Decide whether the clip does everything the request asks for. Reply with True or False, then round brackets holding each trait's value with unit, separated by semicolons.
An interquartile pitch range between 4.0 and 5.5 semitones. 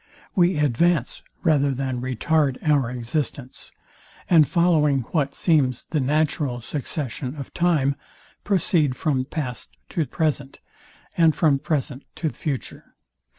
False (3.4 semitones)